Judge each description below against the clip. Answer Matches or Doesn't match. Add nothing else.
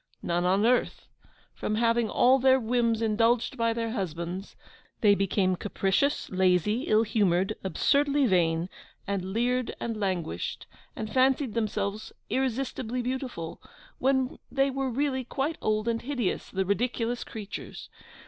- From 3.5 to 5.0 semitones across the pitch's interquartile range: Matches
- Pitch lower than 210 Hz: Doesn't match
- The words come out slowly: Matches